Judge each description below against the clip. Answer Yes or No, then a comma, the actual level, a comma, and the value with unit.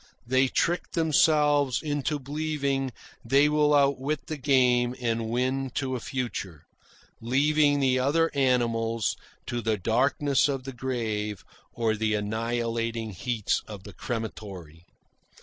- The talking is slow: Yes, slow, 125 wpm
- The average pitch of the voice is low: Yes, low, 130 Hz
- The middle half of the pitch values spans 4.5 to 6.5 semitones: No, average, 3.8 semitones